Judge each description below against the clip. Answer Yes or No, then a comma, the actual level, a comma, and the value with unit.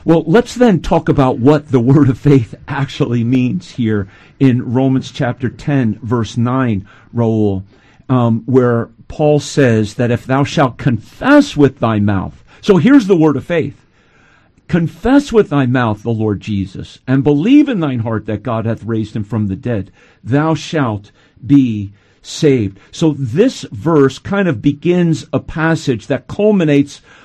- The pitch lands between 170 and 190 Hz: No, low, 135 Hz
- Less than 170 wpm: Yes, average, 160 wpm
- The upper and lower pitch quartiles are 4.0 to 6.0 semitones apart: Yes, average, 5.1 semitones